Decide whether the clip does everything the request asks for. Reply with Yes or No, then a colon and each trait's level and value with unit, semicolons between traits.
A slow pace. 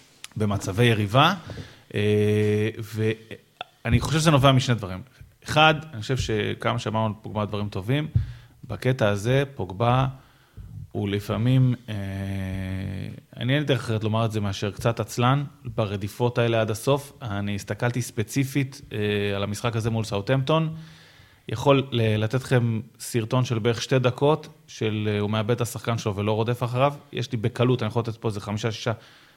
No: average, 145 wpm